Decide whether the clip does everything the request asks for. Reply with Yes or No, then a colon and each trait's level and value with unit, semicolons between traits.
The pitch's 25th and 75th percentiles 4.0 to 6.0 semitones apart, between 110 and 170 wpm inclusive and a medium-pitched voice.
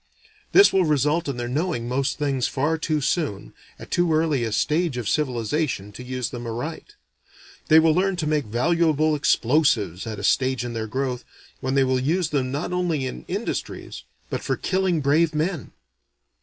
No: average, 4.4 semitones; average, 180 wpm; medium, 145 Hz